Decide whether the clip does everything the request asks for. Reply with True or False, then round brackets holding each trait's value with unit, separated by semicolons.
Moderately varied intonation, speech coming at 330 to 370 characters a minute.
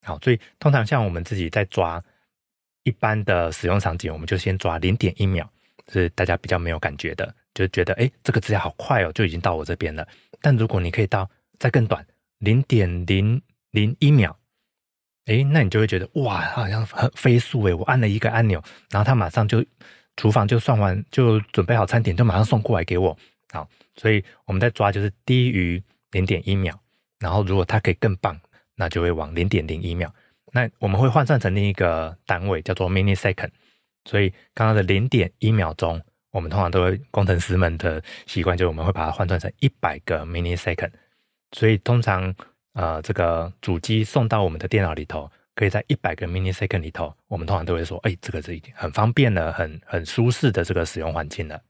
True (4.3 semitones; 335 characters per minute)